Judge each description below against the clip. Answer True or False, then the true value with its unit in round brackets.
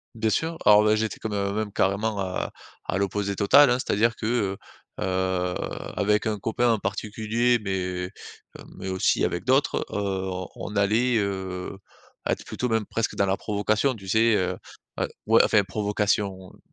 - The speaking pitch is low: True (105 Hz)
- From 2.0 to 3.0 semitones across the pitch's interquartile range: True (2.5 semitones)